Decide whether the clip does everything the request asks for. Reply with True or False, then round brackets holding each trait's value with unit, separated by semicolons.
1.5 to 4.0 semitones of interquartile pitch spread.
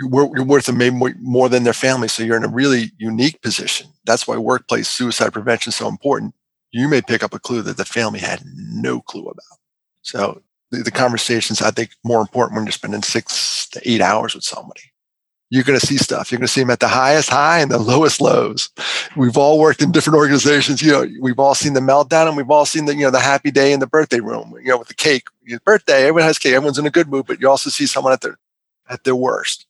True (2.8 semitones)